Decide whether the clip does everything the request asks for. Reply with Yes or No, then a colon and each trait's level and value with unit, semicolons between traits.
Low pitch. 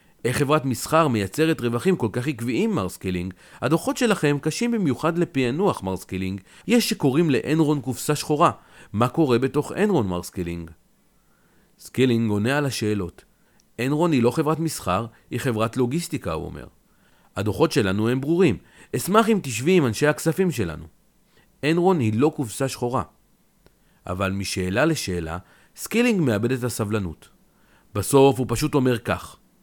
Yes: low, 130 Hz